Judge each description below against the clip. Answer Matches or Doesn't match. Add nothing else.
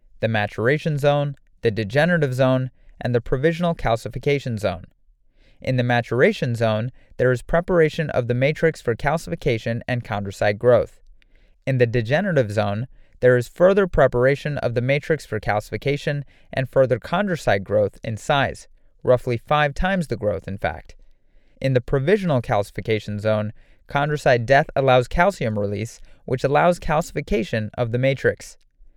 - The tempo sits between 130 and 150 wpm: Matches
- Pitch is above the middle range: Doesn't match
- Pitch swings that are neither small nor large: Matches